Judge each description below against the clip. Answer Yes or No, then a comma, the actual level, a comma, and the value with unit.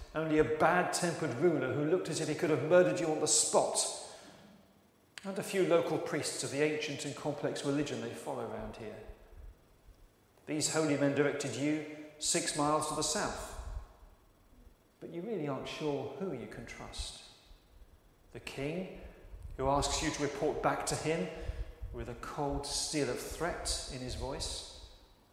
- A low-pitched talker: No, medium, 145 Hz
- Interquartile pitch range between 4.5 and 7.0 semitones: Yes, average, 5.0 semitones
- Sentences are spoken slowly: No, average, 165 wpm